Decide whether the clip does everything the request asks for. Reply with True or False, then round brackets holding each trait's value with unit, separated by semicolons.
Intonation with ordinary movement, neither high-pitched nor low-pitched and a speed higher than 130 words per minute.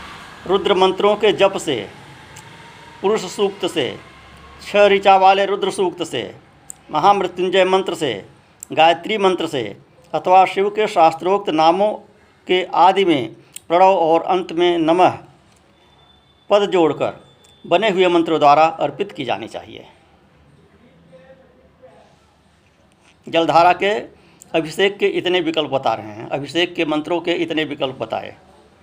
False (3.6 semitones; 180 Hz; 125 wpm)